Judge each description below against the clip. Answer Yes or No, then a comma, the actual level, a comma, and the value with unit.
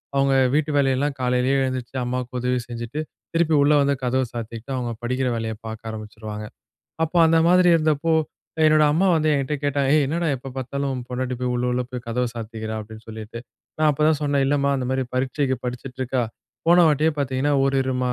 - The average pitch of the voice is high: No, low, 130 Hz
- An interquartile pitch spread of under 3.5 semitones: Yes, average, 2.9 semitones